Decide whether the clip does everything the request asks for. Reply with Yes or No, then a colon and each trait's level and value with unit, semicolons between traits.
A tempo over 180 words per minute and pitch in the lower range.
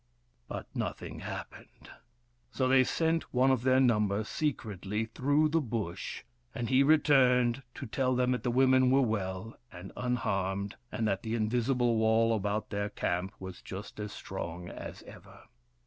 No: average, 155 wpm; low, 115 Hz